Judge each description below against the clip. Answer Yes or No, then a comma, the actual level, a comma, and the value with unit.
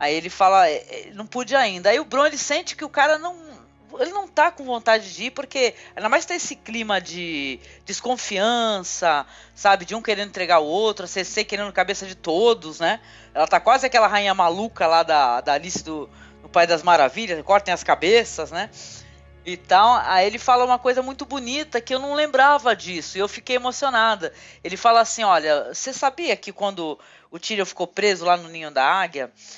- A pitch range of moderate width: No, wide, 6.3 semitones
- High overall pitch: Yes, high, 215 Hz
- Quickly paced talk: Yes, fast, 200 wpm